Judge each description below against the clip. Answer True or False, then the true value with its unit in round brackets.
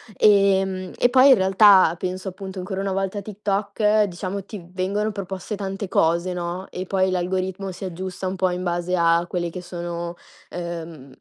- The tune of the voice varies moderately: False (1.9 semitones)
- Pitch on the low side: False (185 Hz)